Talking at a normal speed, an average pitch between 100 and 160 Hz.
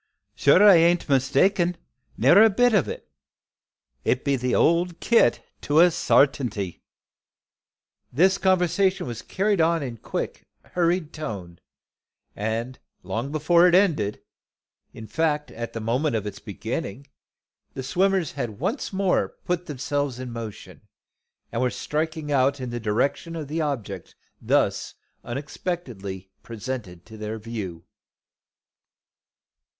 No: slow, 130 wpm; medium, 140 Hz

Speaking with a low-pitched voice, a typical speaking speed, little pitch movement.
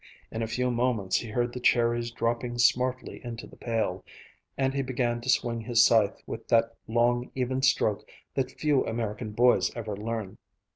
Yes: low, 120 Hz; average, 175 wpm; narrow, 1.7 semitones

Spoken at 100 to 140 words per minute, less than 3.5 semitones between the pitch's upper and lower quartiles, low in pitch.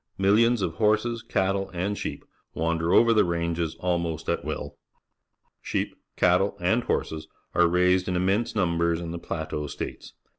Yes: slow, 135 wpm; average, 2.9 semitones; very low, 90 Hz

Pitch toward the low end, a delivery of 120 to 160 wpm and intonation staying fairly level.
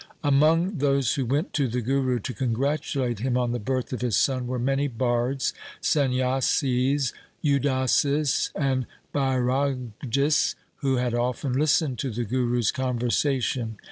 Yes: low, 130 Hz; average, 140 wpm; narrow, 2.2 semitones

